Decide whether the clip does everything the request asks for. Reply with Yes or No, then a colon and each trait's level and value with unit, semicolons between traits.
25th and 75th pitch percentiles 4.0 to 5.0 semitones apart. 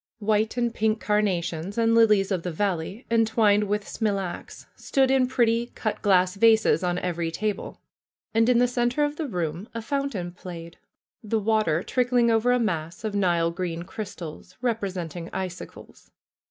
Yes: average, 4.3 semitones